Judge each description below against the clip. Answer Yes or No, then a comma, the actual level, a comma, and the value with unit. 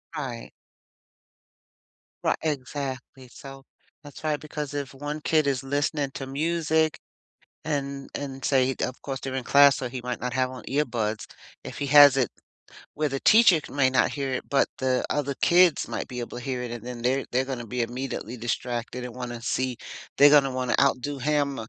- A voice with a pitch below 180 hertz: Yes, low, 135 Hz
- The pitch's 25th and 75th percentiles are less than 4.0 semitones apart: Yes, narrow, 2.4 semitones